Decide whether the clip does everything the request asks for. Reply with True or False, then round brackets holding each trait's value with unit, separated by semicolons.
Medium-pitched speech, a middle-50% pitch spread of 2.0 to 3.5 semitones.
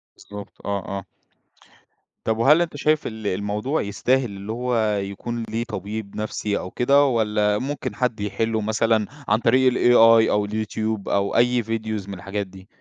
False (110 Hz; 2.8 semitones)